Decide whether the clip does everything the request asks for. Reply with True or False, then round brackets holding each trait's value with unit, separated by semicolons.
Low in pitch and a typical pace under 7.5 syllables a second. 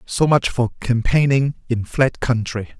True (125 Hz; 4.2 syllables/s)